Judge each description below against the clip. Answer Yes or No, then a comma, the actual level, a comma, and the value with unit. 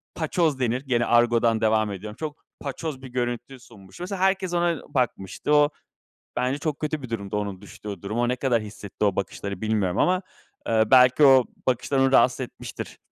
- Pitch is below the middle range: Yes, low, 125 Hz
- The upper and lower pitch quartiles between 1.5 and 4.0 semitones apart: No, average, 4.7 semitones